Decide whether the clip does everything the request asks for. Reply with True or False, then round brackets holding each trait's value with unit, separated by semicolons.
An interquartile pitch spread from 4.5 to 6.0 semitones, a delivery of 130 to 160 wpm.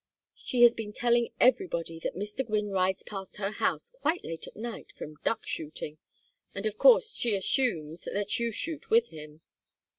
False (4.9 semitones; 175 wpm)